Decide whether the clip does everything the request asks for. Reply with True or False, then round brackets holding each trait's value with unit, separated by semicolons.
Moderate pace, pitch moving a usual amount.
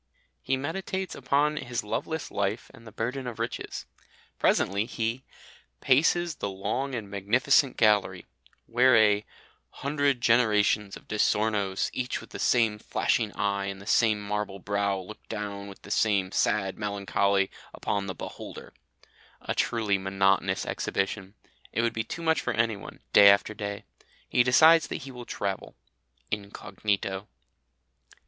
True (145 wpm; 3.7 semitones)